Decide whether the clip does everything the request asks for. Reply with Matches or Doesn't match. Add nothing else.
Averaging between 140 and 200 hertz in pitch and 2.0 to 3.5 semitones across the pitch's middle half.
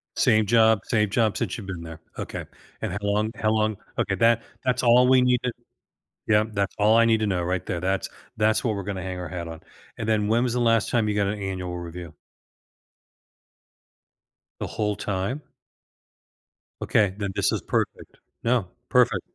Doesn't match